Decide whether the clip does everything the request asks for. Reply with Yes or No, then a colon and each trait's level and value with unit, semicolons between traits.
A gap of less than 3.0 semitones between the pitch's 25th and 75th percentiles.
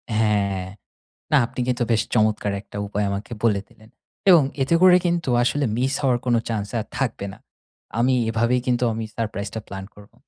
No: average, 3.4 semitones